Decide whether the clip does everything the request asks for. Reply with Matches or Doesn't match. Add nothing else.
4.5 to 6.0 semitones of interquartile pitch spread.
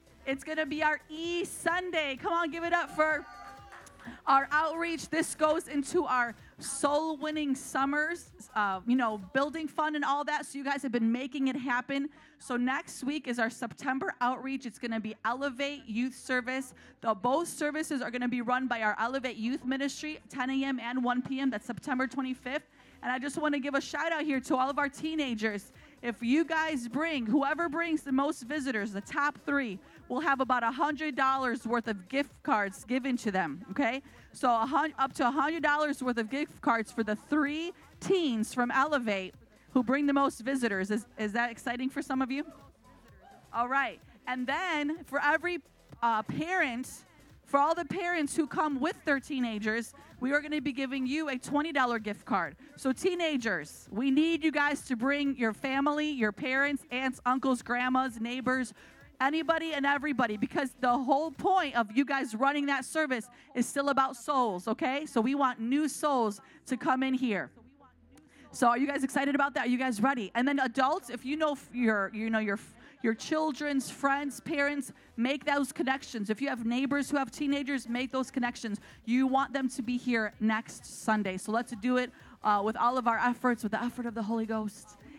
Doesn't match